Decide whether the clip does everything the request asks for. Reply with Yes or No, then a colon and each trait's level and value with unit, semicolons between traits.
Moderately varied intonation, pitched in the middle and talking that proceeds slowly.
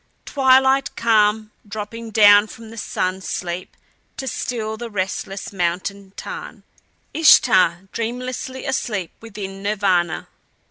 No: average, 3.2 semitones; high, 210 Hz; slow, 105 wpm